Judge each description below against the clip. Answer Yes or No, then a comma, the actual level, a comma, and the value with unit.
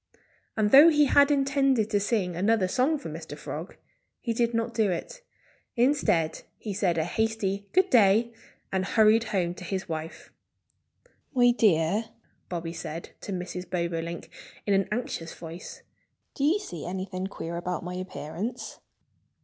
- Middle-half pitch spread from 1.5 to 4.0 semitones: No, average, 5.1 semitones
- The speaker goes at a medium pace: Yes, average, 150 wpm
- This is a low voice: No, high, 200 Hz